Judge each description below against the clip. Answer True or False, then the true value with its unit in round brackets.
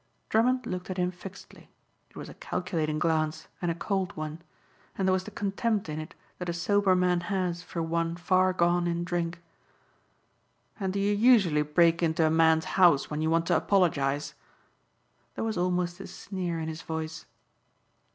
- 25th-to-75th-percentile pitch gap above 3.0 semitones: False (2.5 semitones)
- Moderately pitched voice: True (175 Hz)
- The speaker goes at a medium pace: True (180 wpm)